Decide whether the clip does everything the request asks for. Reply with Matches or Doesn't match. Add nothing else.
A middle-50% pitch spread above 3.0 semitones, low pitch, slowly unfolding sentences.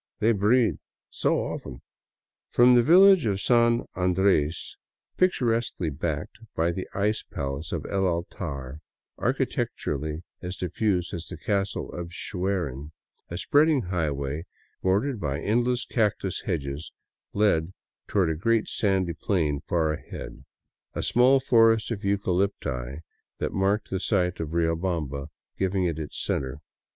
Matches